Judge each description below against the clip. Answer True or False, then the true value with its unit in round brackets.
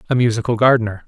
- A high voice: False (115 Hz)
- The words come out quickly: False (170 wpm)